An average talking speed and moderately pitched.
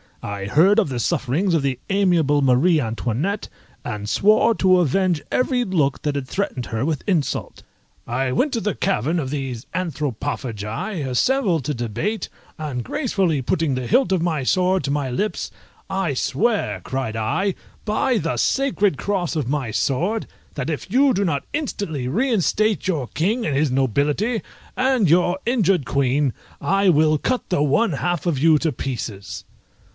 Yes: average, 160 wpm; medium, 160 Hz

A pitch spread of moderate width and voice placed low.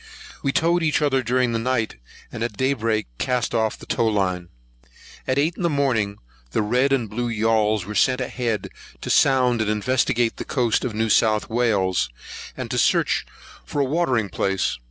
Yes: average, 3.3 semitones; low, 115 Hz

